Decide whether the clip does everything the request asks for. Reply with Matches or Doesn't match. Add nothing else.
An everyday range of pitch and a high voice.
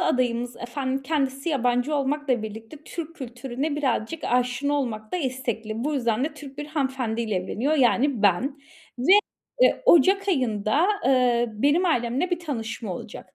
Matches